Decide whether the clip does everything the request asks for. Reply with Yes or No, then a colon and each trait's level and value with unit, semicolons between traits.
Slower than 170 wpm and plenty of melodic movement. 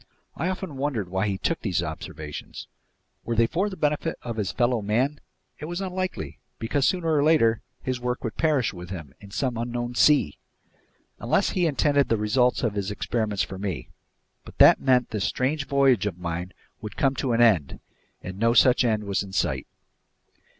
No: average, 185 wpm; wide, 5.7 semitones